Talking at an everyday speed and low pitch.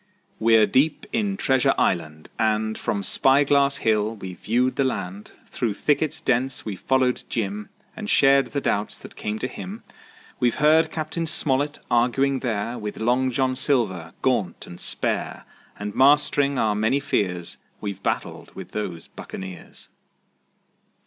Yes: average, 145 wpm; low, 125 Hz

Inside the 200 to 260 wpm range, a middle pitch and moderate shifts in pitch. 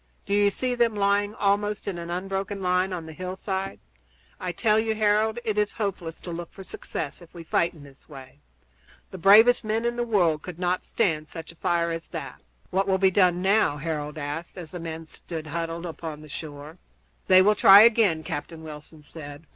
Yes: fast, 205 wpm; medium, 180 Hz; average, 4.0 semitones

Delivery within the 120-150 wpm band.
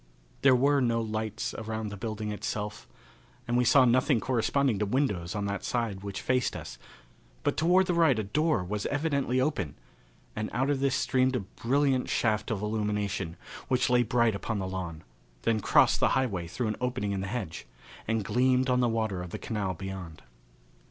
No: average, 185 wpm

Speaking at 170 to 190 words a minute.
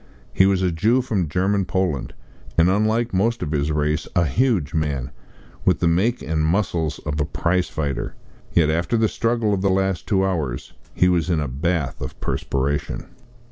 Yes: average, 185 wpm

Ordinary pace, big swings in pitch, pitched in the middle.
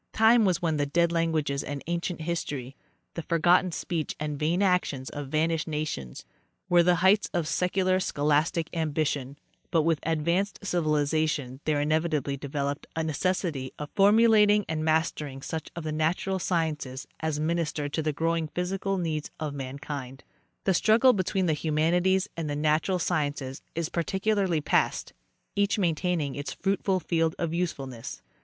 No: average, 145 wpm; average, 3.3 semitones; medium, 160 Hz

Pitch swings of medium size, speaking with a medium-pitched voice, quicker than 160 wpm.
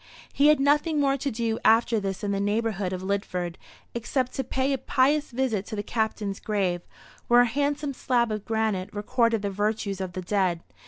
No: average, 4.6 semitones; high, 220 Hz; average, 195 wpm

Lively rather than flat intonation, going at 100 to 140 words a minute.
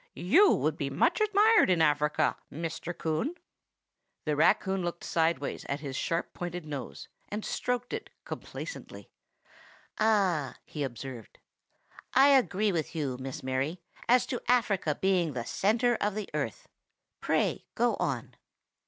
Yes: wide, 6.6 semitones; slow, 135 wpm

